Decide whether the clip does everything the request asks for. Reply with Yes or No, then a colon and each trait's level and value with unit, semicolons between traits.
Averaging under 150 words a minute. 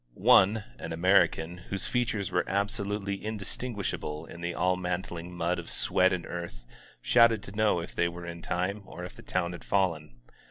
No: average, 175 wpm